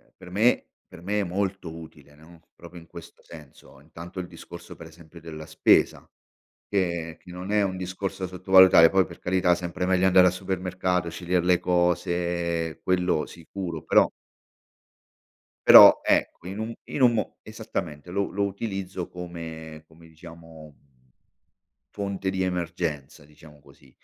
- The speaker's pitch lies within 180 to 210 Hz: No, very low, 90 Hz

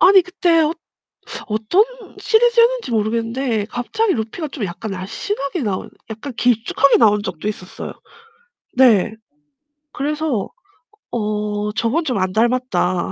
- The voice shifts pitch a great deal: Yes, wide, 6.7 semitones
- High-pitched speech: Yes, high, 235 Hz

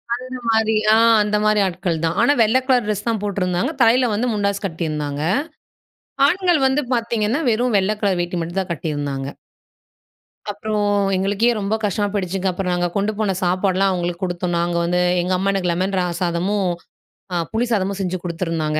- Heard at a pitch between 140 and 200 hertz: Yes, high, 195 Hz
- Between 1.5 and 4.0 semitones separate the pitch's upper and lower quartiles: Yes, average, 3.6 semitones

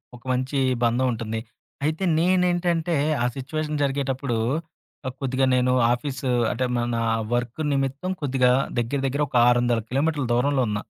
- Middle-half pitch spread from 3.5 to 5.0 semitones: No, average, 3.1 semitones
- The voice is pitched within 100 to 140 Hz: Yes, low, 135 Hz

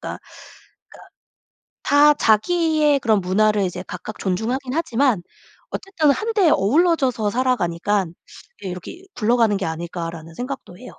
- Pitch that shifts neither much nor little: No, wide, 7.4 semitones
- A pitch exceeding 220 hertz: Yes, high, 230 Hz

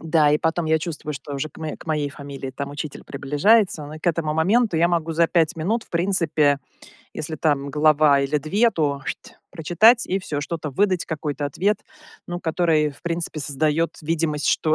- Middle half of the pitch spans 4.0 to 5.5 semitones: No, narrow, 2.6 semitones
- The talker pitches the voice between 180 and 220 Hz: No, medium, 155 Hz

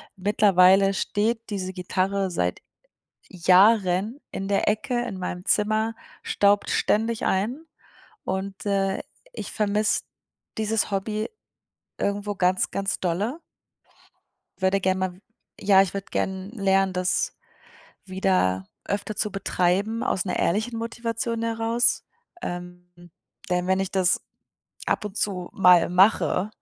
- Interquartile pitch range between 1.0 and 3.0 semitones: Yes, narrow, 2.5 semitones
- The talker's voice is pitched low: No, high, 195 Hz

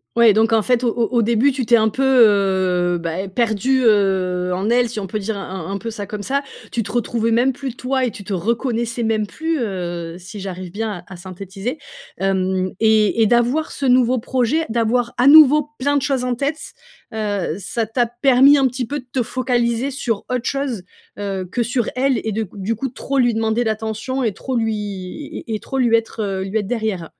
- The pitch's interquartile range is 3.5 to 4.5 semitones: Yes, average, 3.9 semitones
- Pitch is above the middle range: Yes, high, 225 Hz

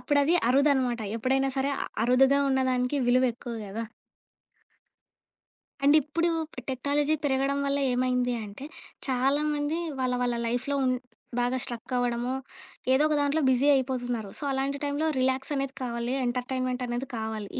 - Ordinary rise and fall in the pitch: No, narrow, 2.2 semitones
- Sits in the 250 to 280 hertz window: Yes, very high, 260 Hz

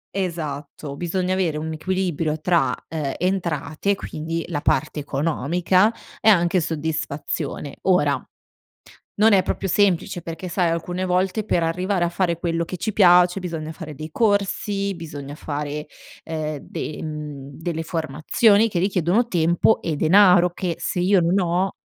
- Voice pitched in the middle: Yes, medium, 170 Hz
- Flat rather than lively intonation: No, average, 3.1 semitones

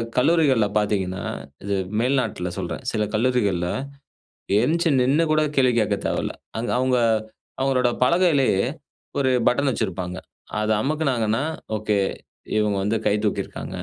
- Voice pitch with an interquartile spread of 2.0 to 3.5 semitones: No, average, 4.6 semitones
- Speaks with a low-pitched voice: Yes, low, 125 Hz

